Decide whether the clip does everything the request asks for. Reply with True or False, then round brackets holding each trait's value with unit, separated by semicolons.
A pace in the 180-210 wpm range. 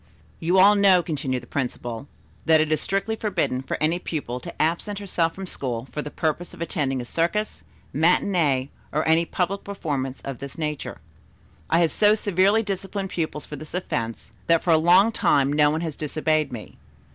True (185 wpm)